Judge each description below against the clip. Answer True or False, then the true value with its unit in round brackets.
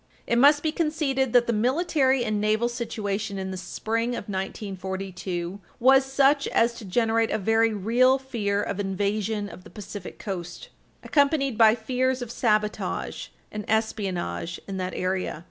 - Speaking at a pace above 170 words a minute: False (155 wpm)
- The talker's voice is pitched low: False (220 Hz)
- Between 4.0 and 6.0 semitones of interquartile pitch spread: True (4.4 semitones)